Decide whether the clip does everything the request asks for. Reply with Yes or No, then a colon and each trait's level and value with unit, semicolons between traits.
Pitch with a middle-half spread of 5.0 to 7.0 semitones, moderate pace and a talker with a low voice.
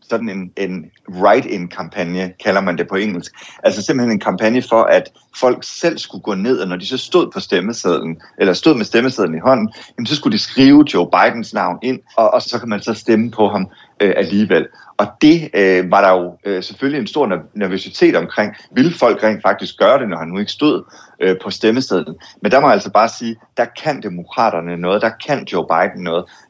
Yes: average, 5.3 semitones; average, 200 wpm; low, 105 Hz